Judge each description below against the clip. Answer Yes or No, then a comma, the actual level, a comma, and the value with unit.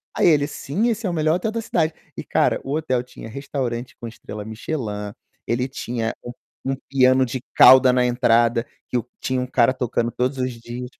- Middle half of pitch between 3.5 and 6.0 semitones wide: No, average, 2.9 semitones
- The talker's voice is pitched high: No, low, 125 Hz